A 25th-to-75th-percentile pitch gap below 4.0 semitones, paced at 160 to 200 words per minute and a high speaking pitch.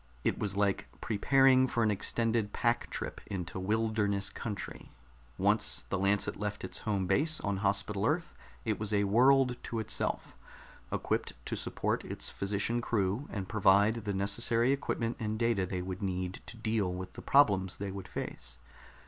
No: average, 3.0 semitones; average, 165 wpm; low, 105 Hz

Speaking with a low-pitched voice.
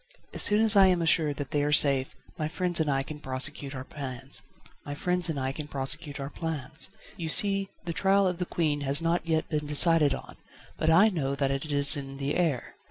No: medium, 150 Hz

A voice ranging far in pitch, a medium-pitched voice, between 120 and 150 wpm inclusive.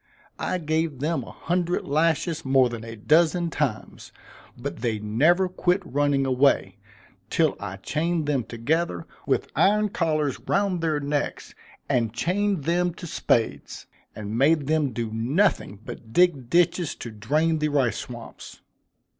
Yes: wide, 5.9 semitones; medium, 150 Hz; average, 145 wpm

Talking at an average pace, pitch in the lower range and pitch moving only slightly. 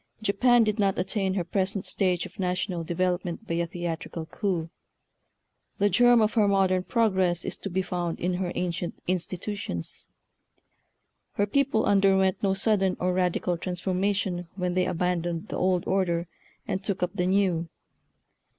No: average, 155 wpm; medium, 185 Hz; narrow, 2.1 semitones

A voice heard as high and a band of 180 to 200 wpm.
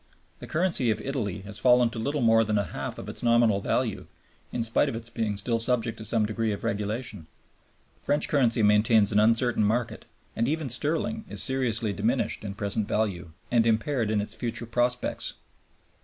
No: low, 115 Hz; average, 185 wpm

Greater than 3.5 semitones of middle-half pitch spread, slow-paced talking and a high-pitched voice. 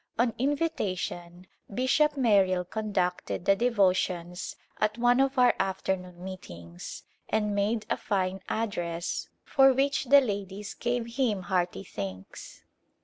Yes: average, 4.9 semitones; slow, 120 wpm; high, 200 Hz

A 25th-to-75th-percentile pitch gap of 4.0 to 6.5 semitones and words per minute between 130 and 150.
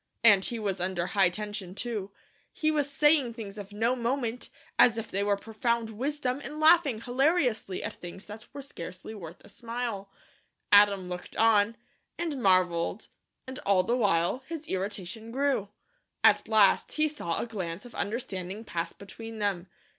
No: average, 4.3 semitones; average, 160 wpm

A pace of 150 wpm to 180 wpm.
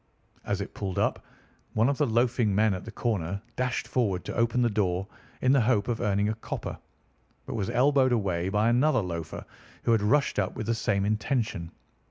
No: average, 200 wpm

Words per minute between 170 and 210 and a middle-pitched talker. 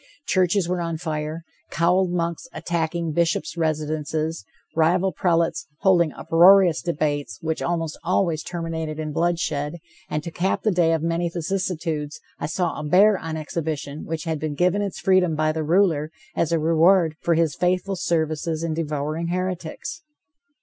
No: average, 155 wpm; medium, 165 Hz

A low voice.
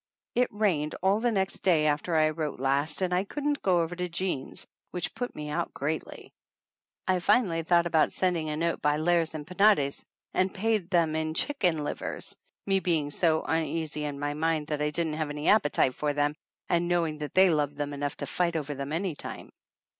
No: medium, 160 Hz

